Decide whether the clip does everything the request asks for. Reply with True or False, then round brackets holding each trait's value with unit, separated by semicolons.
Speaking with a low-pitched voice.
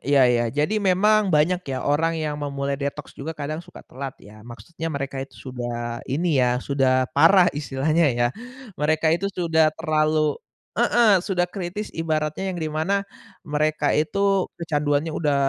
False (155 Hz)